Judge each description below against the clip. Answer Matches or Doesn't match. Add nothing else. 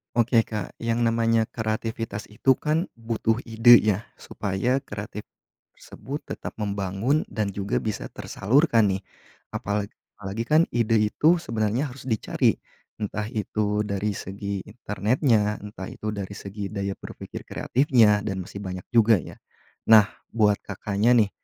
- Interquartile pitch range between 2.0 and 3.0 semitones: Matches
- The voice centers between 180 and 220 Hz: Doesn't match